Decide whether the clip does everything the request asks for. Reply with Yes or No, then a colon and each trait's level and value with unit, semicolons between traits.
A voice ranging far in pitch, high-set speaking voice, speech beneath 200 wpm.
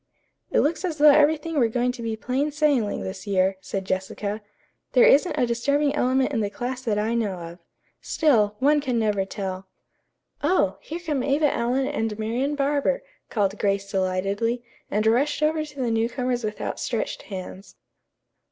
Yes: wide, 5.8 semitones; high, 235 Hz; average, 170 wpm